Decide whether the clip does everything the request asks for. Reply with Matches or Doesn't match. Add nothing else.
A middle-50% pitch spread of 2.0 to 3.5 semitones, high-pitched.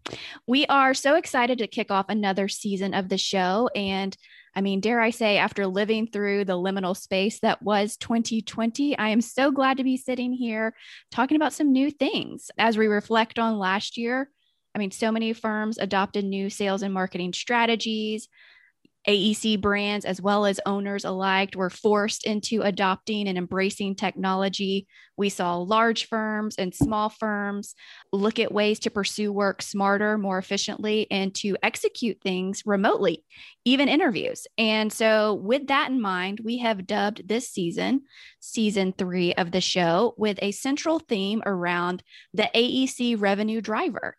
Matches